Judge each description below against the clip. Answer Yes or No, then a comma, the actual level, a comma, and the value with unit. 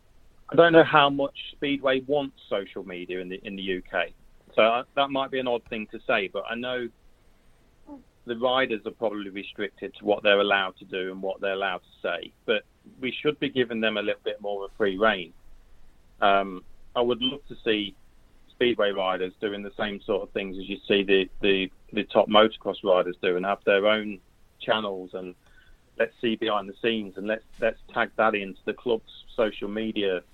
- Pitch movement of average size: Yes, average, 4.1 semitones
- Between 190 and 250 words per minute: Yes, average, 200 wpm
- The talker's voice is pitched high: No, low, 105 Hz